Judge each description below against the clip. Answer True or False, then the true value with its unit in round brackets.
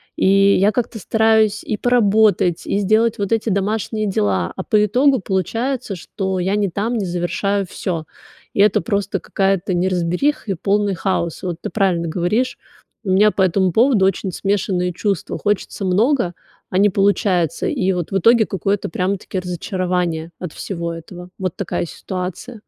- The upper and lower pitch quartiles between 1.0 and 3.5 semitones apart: True (2.8 semitones)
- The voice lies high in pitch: True (195 Hz)